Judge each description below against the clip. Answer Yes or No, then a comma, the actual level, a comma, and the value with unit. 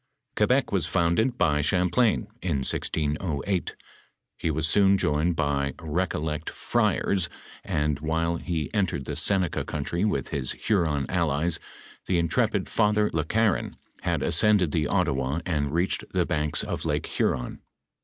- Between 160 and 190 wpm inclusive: No, slow, 135 wpm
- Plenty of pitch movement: No, average, 3.9 semitones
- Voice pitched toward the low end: Yes, very low, 85 Hz